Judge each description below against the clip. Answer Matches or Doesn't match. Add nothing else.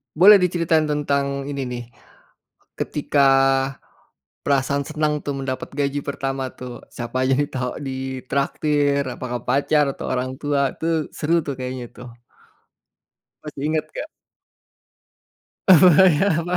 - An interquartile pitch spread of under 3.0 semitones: Matches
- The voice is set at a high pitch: Doesn't match